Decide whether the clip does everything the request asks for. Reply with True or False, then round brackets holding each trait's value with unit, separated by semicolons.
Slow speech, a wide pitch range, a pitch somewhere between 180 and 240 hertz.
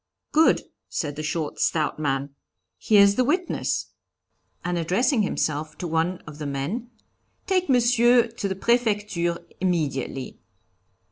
True (125 wpm; 7.5 semitones; 185 Hz)